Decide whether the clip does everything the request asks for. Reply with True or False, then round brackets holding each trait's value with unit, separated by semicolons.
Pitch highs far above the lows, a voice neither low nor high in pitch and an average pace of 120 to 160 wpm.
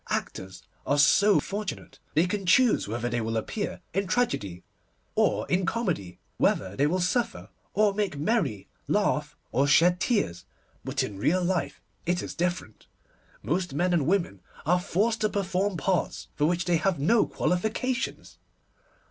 True (6.0 semitones; 180 Hz; 155 wpm)